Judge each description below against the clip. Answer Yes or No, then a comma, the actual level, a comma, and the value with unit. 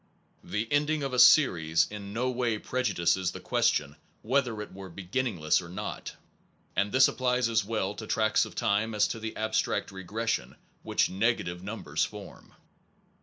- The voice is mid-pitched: No, low, 110 Hz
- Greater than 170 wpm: No, average, 160 wpm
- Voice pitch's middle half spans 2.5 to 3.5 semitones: No, average, 4.2 semitones